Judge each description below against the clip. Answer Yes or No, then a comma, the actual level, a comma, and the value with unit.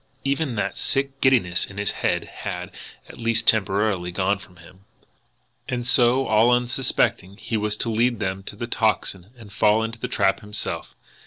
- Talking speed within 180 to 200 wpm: No, average, 170 wpm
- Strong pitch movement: No, average, 3.5 semitones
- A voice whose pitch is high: No, low, 110 Hz